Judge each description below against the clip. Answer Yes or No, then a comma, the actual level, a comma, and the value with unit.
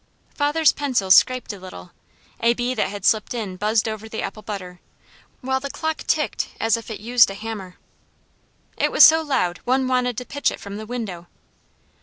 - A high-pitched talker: Yes, high, 225 Hz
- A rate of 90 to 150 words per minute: No, average, 190 wpm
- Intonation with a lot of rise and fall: No, average, 4.1 semitones